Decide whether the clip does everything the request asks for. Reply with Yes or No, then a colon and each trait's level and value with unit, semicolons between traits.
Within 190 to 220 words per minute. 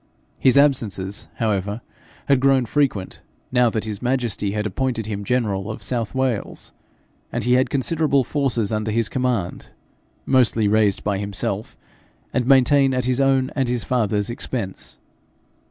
No: average, 145 wpm